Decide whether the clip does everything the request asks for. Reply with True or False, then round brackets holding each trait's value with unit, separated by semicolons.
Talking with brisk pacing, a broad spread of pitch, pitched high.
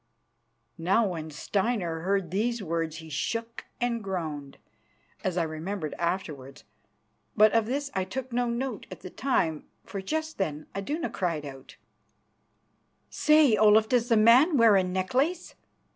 False (145 wpm; 6.3 semitones; 200 Hz)